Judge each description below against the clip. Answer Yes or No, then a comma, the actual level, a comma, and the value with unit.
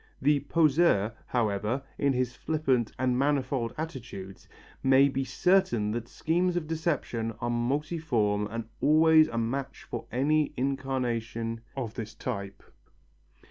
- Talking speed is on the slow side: Yes, slow, 125 wpm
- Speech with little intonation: No, average, 4.6 semitones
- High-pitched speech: No, low, 130 Hz